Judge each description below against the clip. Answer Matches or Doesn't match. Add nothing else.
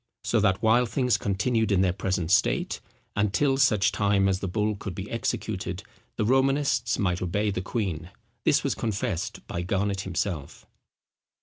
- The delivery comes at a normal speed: Matches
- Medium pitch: Doesn't match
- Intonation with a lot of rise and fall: Doesn't match